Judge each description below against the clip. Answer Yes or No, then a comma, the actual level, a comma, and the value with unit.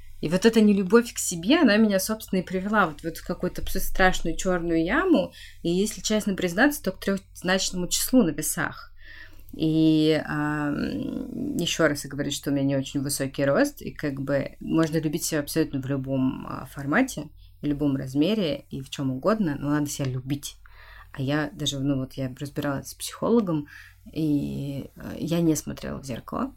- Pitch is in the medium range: Yes, medium, 155 Hz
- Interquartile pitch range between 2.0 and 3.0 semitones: No, average, 5.2 semitones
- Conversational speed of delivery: No, fast, 175 wpm